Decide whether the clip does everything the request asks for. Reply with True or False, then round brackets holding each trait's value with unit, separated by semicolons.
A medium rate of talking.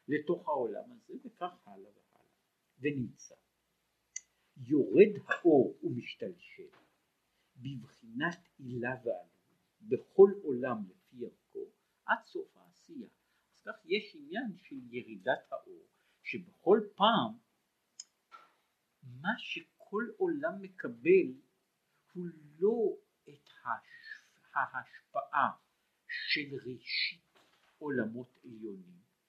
False (85 wpm)